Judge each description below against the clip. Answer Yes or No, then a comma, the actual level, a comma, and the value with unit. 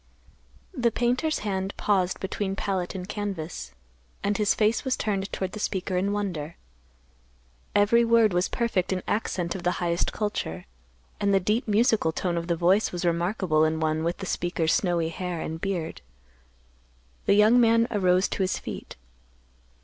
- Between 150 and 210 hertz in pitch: Yes, high, 190 Hz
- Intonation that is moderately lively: Yes, average, 3.3 semitones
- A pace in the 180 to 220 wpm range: No, average, 165 wpm